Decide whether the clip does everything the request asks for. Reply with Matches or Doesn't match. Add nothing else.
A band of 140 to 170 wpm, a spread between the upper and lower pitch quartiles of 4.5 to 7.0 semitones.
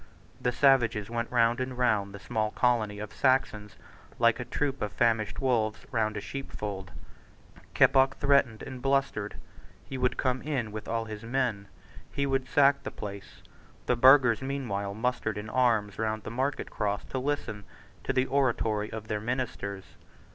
Doesn't match